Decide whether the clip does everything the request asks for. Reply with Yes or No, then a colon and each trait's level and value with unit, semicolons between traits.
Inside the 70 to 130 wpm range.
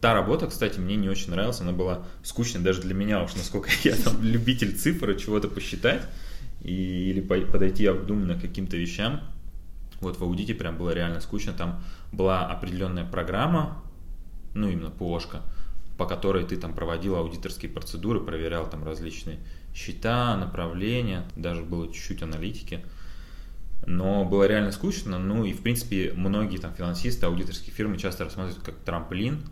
No: average, 150 wpm